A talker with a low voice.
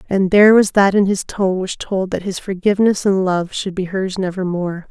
No: high, 190 Hz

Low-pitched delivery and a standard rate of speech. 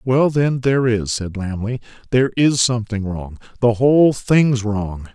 Yes: low, 115 Hz; average, 165 wpm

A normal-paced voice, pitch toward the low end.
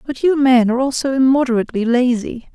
No: average, 190 wpm; very high, 255 Hz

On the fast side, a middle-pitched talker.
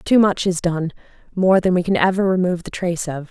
Yes: fast, 220 wpm; medium, 180 Hz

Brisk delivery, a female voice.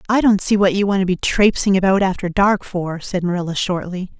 Yes: fast, 230 wpm; female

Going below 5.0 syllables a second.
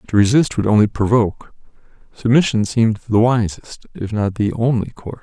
No: 5.4 syllables/s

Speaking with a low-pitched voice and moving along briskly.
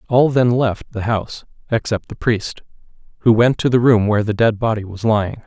Yes: low, 115 Hz; fast, 210 wpm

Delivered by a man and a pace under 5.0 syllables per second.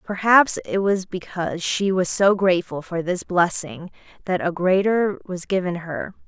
No: female; 4.5 syllables/s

